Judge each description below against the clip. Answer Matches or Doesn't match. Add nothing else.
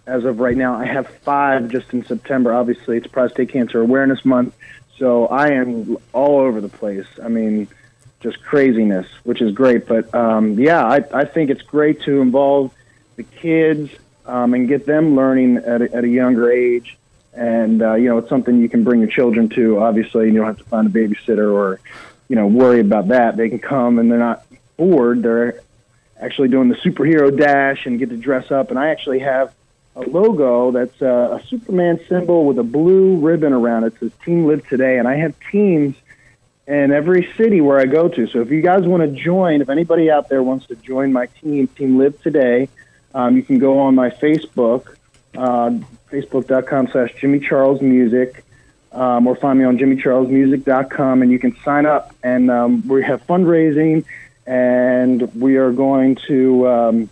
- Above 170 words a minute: Matches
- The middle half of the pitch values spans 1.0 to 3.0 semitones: Matches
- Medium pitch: Doesn't match